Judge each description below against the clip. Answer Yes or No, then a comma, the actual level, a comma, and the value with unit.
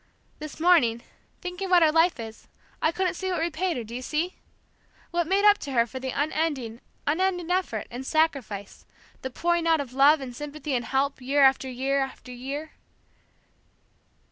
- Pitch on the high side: Yes, very high, 290 Hz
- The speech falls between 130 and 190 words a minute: Yes, average, 175 wpm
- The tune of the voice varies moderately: Yes, average, 4.9 semitones